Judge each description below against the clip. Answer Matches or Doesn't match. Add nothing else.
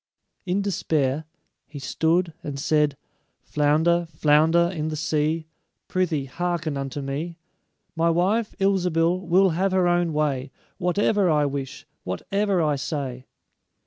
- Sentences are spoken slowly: Matches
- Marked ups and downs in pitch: Doesn't match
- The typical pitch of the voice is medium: Matches